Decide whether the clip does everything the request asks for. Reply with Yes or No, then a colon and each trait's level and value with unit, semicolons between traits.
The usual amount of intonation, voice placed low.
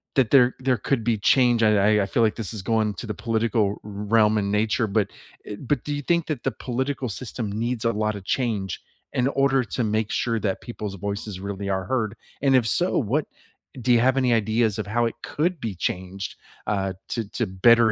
Yes: average, 3.4 semitones; low, 110 Hz